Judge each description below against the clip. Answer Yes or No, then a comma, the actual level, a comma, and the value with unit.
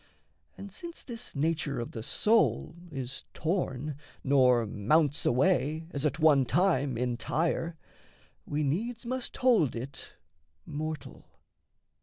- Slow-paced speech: Yes, slow, 115 wpm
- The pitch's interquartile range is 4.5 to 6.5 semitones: Yes, average, 5.0 semitones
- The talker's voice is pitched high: No, medium, 150 Hz